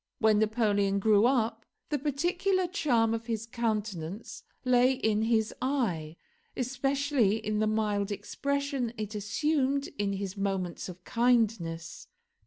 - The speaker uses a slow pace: Yes, slow, 125 wpm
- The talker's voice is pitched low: No, high, 225 Hz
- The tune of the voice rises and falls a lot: No, average, 4.4 semitones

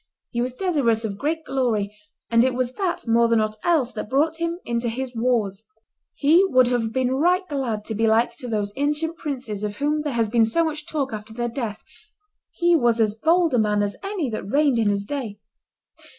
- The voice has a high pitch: Yes, high, 245 Hz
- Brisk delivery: Yes, fast, 210 wpm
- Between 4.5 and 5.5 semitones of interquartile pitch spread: Yes, average, 5.2 semitones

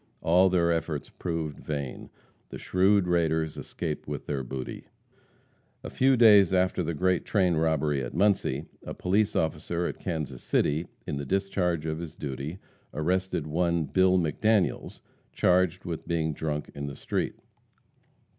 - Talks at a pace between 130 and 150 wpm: Yes, average, 145 wpm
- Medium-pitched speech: No, very low, 85 Hz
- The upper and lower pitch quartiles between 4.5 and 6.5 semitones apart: No, average, 3.4 semitones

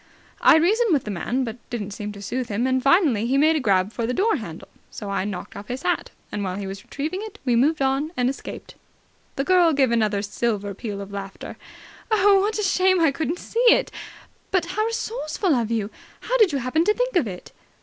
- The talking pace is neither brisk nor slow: No, fast, 225 wpm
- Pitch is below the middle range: No, very high, 265 Hz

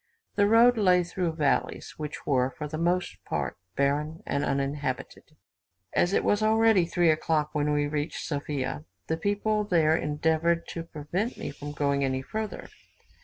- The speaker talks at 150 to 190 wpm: Yes, average, 160 wpm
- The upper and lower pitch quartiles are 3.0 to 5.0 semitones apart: Yes, average, 3.8 semitones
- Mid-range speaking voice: Yes, medium, 155 Hz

